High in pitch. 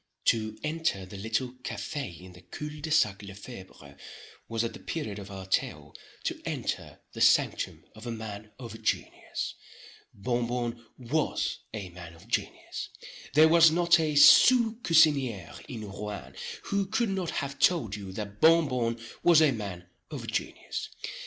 No: low, 115 Hz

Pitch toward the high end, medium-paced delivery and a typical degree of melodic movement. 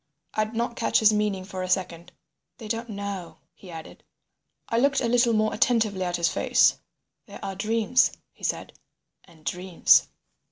Yes: high, 205 Hz; average, 170 wpm; average, 3.9 semitones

